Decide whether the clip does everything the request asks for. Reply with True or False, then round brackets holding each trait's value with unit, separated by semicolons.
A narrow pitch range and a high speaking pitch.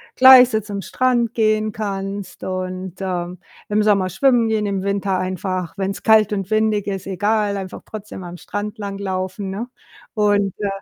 True (2.2 semitones; 200 Hz)